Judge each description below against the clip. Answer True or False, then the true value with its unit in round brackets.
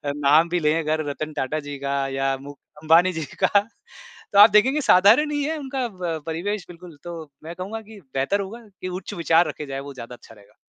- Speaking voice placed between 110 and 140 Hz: False (170 Hz)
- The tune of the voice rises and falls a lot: True (5.7 semitones)